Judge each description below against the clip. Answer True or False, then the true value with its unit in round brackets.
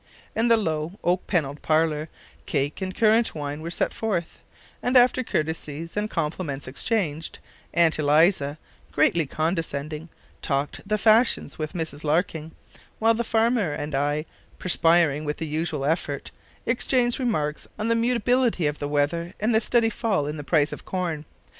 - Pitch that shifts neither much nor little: False (6.4 semitones)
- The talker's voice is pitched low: False (165 Hz)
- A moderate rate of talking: True (155 wpm)